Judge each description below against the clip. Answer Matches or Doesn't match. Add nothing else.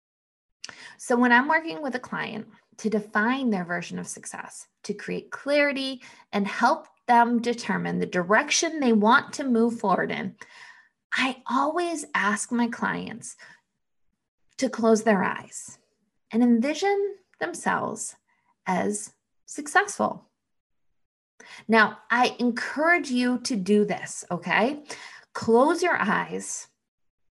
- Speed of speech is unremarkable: Doesn't match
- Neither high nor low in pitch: Doesn't match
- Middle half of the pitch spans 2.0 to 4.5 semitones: Doesn't match